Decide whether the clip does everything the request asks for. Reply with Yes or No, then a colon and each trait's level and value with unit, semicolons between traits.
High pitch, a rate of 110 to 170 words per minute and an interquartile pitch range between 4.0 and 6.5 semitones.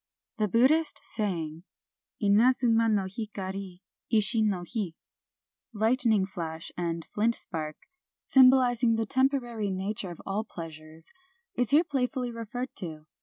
Yes: high, 215 Hz; slow, 135 wpm; average, 4.8 semitones